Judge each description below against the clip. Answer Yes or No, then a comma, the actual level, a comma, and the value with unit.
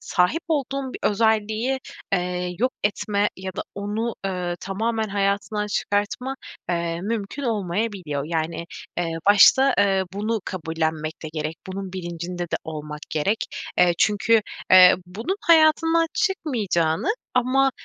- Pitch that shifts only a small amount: No, average, 4.7 semitones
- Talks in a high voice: Yes, high, 200 Hz